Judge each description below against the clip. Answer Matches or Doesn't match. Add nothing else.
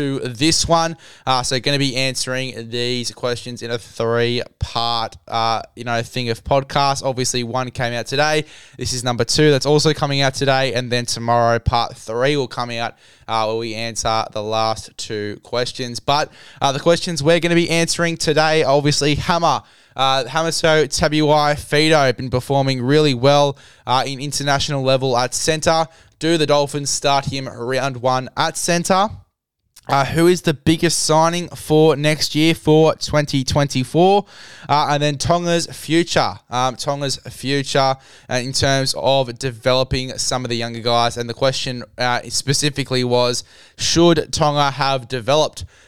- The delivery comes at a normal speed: Matches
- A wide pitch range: Doesn't match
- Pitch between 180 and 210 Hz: Doesn't match